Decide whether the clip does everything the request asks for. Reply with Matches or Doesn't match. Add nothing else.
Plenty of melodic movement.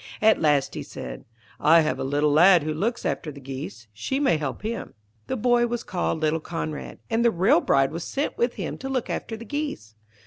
Matches